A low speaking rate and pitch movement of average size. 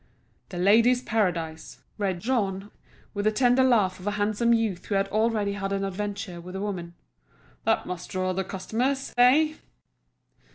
No: average, 155 wpm; average, 3.5 semitones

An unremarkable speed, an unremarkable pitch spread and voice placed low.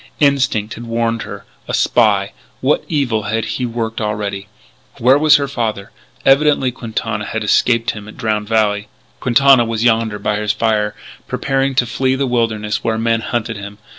Yes: average, 165 wpm; average, 3.0 semitones; low, 115 Hz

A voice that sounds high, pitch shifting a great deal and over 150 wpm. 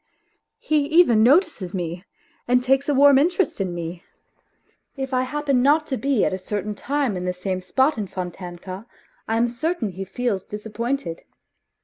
Yes: high, 235 Hz; wide, 6.9 semitones; average, 165 wpm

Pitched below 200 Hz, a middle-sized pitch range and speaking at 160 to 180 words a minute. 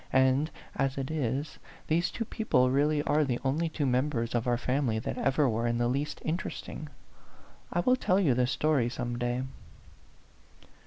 Yes: low, 135 Hz; average, 4.0 semitones; average, 170 wpm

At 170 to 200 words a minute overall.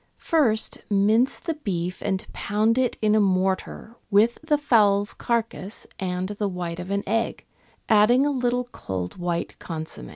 No: average, 150 wpm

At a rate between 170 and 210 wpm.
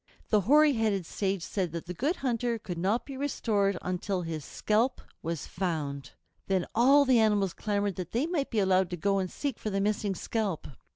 Yes: average, 195 wpm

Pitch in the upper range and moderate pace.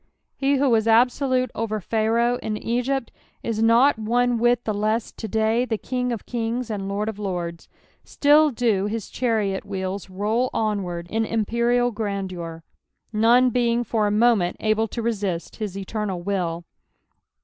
Yes: high, 220 Hz; average, 155 wpm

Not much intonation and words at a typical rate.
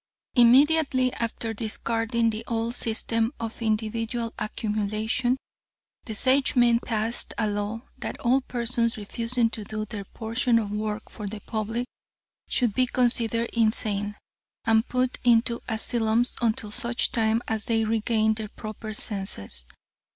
No: narrow, 1.6 semitones; slow, 130 wpm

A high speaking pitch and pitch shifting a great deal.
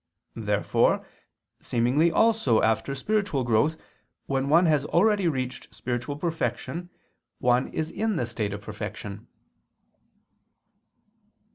No: low, 135 Hz; wide, 6.0 semitones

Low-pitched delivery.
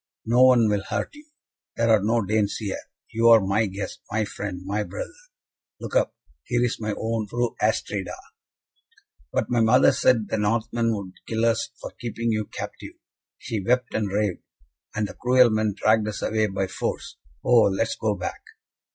Yes: low, 110 Hz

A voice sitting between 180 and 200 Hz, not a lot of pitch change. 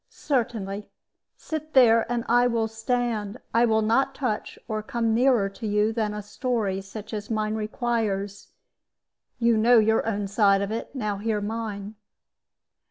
No: high, 220 Hz; narrow, 2.2 semitones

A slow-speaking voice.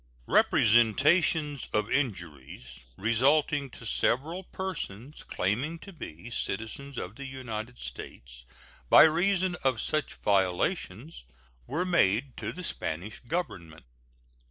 Yes: slow, 110 wpm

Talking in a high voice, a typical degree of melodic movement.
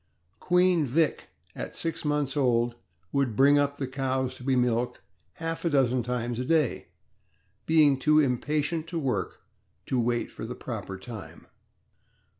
No: low, 135 Hz; average, 3.7 semitones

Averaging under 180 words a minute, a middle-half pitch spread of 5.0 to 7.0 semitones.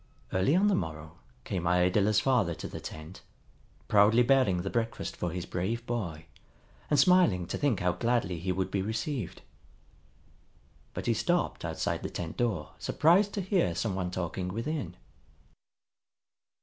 Yes: average, 150 wpm; wide, 5.4 semitones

